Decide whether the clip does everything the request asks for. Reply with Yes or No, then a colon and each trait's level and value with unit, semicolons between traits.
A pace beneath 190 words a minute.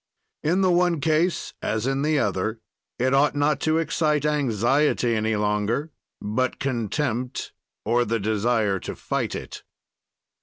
Yes: average, 140 wpm